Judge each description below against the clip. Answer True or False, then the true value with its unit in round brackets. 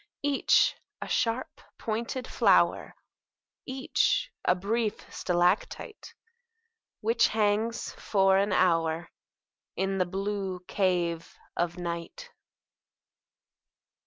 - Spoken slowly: True (85 wpm)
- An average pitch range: True (4.4 semitones)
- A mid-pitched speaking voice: False (195 Hz)